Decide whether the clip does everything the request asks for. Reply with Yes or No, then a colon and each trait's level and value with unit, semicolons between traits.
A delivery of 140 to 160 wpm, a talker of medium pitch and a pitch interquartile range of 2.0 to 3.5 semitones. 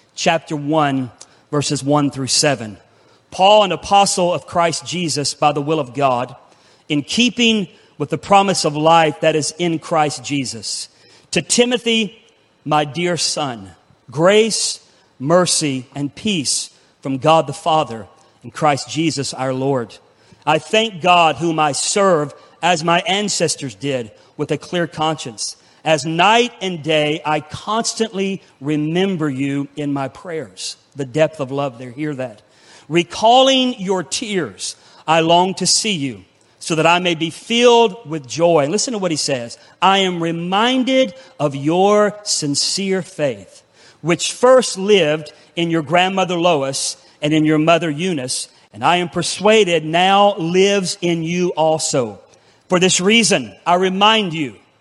No: average, 145 wpm; medium, 160 Hz; average, 4.4 semitones